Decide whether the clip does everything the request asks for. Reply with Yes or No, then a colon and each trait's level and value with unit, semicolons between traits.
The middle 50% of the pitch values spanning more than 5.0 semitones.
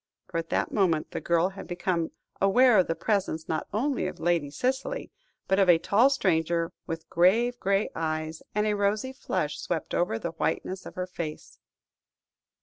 No: average, 4.2 semitones